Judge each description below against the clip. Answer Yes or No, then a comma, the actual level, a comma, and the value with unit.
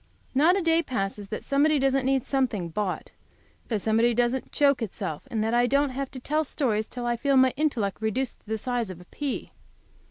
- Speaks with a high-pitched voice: Yes, very high, 250 Hz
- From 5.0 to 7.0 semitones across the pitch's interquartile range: No, average, 4.0 semitones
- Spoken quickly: Yes, fast, 215 wpm